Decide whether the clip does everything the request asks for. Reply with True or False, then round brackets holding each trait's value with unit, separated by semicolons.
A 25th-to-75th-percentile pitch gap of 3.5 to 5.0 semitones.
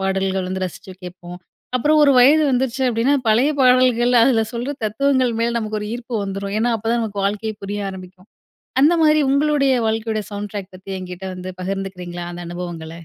True (4.7 semitones)